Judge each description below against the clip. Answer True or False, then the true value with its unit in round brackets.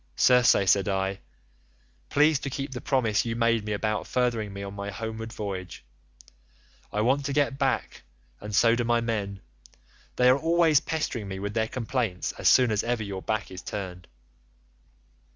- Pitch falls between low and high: False (110 Hz)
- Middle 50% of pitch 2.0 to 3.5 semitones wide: False (4.1 semitones)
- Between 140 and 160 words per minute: False (170 wpm)